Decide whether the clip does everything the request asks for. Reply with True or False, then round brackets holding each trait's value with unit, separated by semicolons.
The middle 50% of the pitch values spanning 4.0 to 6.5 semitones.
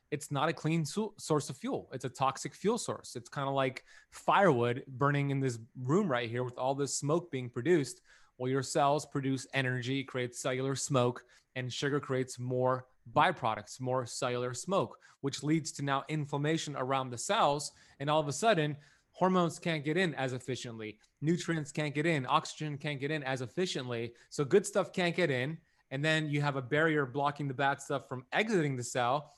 False (3.2 semitones)